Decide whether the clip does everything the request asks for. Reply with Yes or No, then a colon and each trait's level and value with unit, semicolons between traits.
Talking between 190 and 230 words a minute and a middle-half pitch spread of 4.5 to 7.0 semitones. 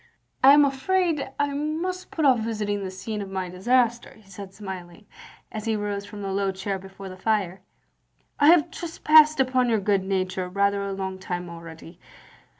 Yes: average, 195 wpm; wide, 5.6 semitones